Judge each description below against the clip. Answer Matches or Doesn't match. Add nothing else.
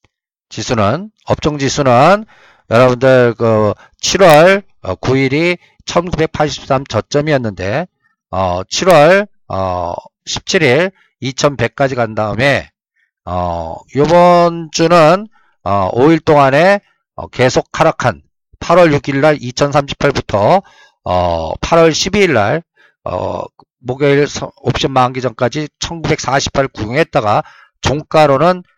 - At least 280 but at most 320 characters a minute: Doesn't match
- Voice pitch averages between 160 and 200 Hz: Doesn't match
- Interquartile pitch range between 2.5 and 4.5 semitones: Doesn't match